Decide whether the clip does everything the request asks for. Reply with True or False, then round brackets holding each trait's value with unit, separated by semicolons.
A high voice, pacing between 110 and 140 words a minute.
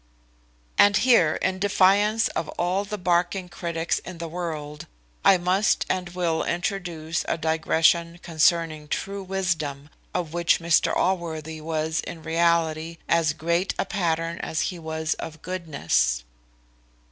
False (170 Hz; 135 wpm)